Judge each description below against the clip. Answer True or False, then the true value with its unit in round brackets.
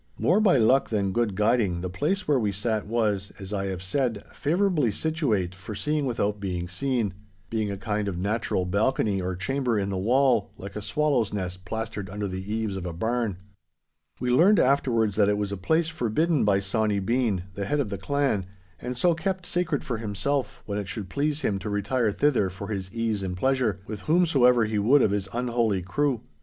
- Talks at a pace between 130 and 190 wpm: False (200 wpm)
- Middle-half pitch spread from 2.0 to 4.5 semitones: False (5.0 semitones)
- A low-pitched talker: True (110 Hz)